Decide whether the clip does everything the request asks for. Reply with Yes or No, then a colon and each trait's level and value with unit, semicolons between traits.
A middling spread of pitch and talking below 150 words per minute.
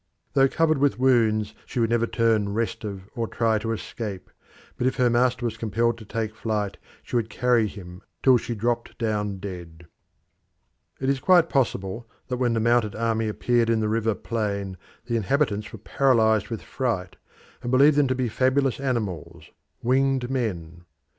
No: average, 3.0 semitones; average, 175 wpm